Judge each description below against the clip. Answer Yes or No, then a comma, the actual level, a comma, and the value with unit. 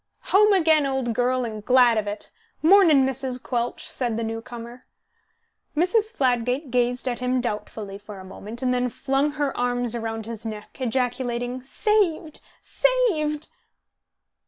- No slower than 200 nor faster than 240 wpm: No, average, 145 wpm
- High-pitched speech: Yes, very high, 250 Hz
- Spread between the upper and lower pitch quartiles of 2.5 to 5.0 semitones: Yes, average, 3.8 semitones